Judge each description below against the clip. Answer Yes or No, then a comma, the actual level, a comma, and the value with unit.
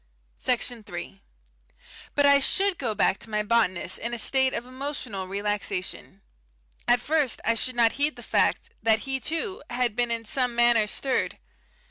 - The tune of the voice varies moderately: Yes, average, 3.9 semitones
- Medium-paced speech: Yes, average, 165 wpm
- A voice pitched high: Yes, high, 240 Hz